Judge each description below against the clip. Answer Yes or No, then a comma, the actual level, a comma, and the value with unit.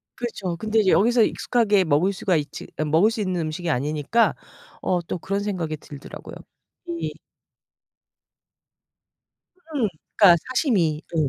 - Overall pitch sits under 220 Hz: Yes, medium, 185 Hz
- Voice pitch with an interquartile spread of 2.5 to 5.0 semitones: No, wide, 5.6 semitones